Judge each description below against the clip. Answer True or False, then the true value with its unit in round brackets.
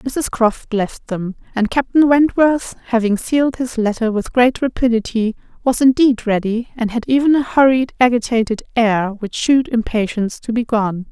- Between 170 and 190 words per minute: False (160 wpm)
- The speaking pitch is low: False (235 Hz)